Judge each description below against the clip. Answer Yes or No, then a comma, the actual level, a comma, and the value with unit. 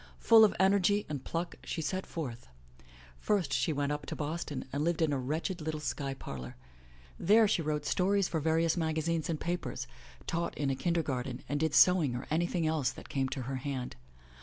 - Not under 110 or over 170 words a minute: No, average, 200 wpm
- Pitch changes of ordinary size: Yes, average, 3.8 semitones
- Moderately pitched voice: Yes, medium, 155 Hz